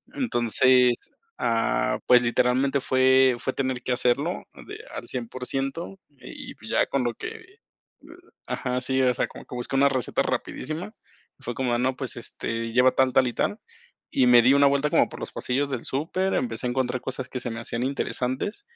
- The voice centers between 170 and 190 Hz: No, low, 130 Hz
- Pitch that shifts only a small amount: Yes, narrow, 1.8 semitones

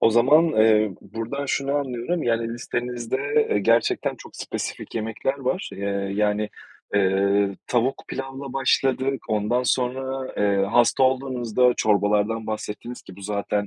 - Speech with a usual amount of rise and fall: Yes, average, 4.1 semitones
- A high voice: No, low, 120 Hz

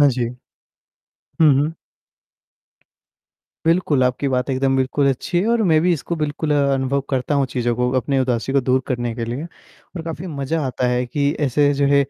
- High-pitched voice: No, medium, 140 Hz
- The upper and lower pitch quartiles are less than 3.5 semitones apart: Yes, average, 2.8 semitones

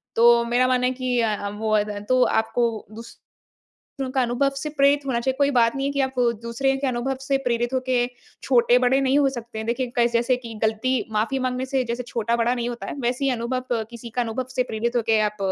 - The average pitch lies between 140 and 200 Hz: No, high, 245 Hz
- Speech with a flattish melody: Yes, narrow, 2.0 semitones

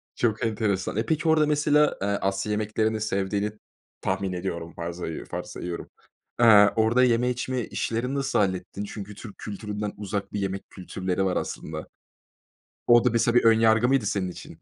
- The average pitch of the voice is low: Yes, low, 105 Hz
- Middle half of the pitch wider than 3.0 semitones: Yes, average, 3.4 semitones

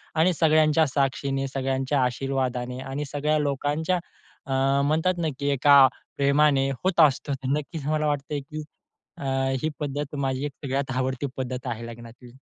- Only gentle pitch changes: Yes, narrow, 2.2 semitones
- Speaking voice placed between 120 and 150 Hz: Yes, medium, 140 Hz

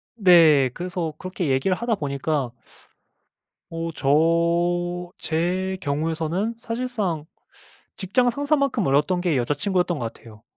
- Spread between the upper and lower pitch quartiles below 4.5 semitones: Yes, average, 4.1 semitones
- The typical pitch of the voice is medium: Yes, medium, 175 Hz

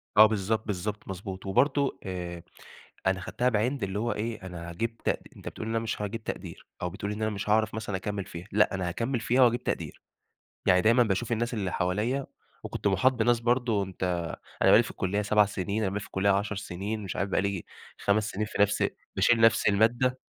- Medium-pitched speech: No, low, 105 Hz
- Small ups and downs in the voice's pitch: No, average, 3.0 semitones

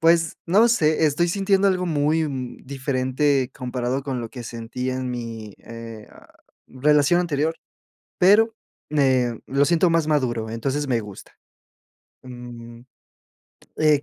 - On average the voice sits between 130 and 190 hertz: Yes, medium, 140 Hz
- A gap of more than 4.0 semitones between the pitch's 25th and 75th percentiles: Yes, average, 4.7 semitones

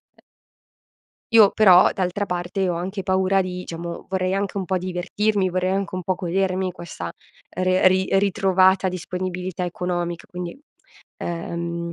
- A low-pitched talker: No, medium, 185 Hz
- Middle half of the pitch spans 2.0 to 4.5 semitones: No, narrow, 1.3 semitones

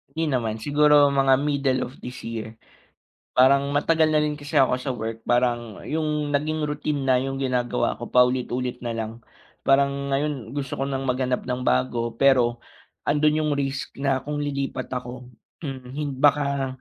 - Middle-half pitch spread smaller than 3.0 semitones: Yes, narrow, 2.6 semitones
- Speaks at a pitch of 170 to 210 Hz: No, low, 135 Hz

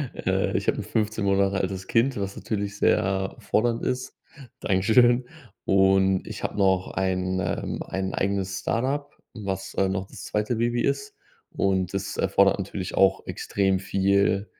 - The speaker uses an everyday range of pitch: No, narrow, 2.2 semitones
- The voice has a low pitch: Yes, low, 100 Hz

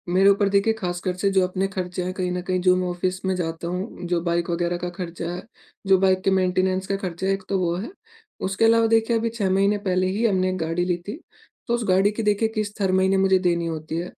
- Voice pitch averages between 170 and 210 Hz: Yes, medium, 185 Hz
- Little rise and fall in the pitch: Yes, narrow, 1.8 semitones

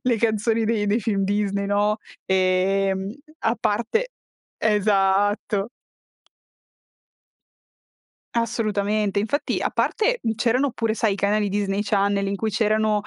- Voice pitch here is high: Yes, high, 210 Hz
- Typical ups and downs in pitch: No, narrow, 2.0 semitones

